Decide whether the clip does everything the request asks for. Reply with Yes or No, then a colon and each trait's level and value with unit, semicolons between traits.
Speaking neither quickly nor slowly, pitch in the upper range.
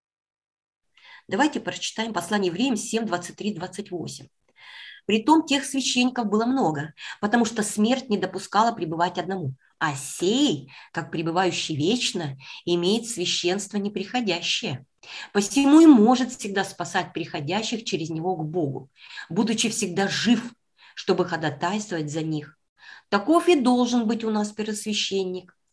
Yes: average, 120 wpm; high, 200 Hz